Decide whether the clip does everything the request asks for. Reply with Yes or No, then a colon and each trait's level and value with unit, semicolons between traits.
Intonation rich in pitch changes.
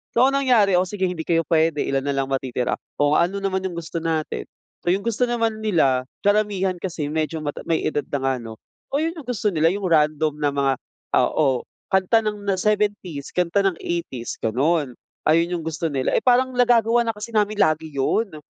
Yes: wide, 5.7 semitones